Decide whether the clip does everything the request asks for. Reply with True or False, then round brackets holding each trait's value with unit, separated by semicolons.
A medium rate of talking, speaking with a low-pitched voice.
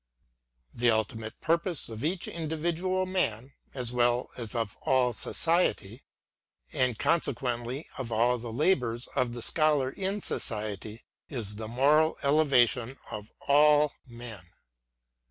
False (120 wpm; 125 Hz)